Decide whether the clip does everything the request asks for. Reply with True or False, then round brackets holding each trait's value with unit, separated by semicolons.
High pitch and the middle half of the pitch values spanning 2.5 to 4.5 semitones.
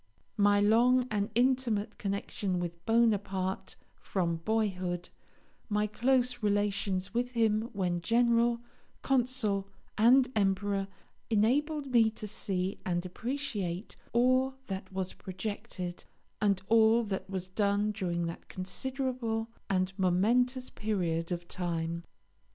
True (205 Hz; 4.1 semitones)